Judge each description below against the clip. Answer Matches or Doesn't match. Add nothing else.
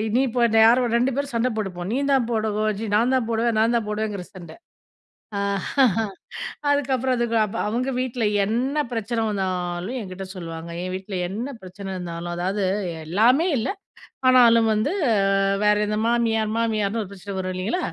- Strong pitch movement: Doesn't match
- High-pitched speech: Matches